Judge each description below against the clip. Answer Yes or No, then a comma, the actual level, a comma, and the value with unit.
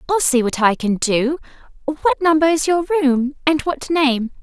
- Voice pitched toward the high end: Yes, very high, 285 Hz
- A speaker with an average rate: Yes, average, 190 wpm